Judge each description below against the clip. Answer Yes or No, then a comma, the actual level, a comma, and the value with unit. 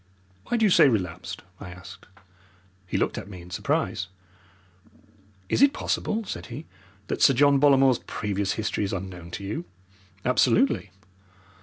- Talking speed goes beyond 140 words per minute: Yes, average, 150 wpm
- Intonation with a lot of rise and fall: Yes, wide, 7.3 semitones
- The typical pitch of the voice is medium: No, low, 105 Hz